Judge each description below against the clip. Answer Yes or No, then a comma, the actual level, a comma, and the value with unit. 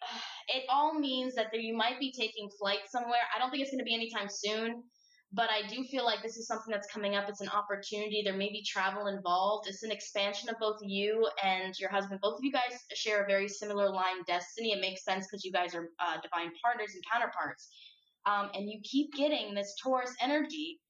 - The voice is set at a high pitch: Yes, high, 210 Hz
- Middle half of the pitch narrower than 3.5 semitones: Yes, average, 3.1 semitones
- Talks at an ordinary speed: No, fast, 225 wpm